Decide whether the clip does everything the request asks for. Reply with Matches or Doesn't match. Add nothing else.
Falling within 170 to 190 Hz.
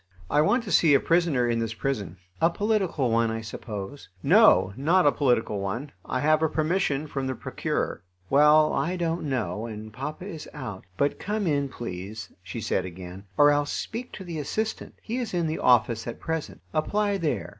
Doesn't match